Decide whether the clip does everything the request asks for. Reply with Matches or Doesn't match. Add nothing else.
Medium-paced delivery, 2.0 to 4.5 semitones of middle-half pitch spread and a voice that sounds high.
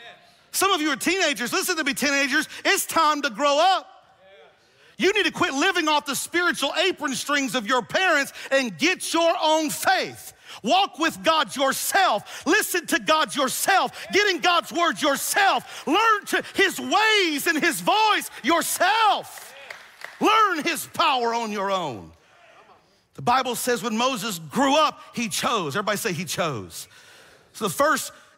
Doesn't match